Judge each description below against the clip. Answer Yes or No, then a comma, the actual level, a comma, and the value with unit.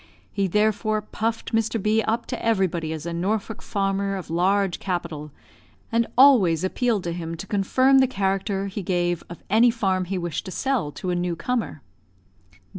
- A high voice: Yes, high, 195 Hz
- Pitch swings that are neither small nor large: Yes, average, 4.1 semitones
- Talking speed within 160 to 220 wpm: Yes, average, 175 wpm